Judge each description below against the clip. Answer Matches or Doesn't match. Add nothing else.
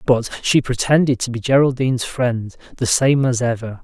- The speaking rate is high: Doesn't match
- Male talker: Matches